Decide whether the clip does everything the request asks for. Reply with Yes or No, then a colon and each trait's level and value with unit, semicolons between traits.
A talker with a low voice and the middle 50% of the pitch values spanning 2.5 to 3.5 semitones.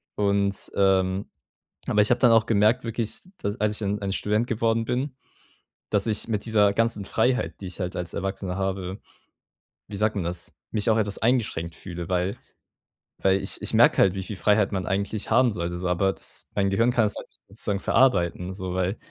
Yes: low, 100 Hz; average, 2.8 semitones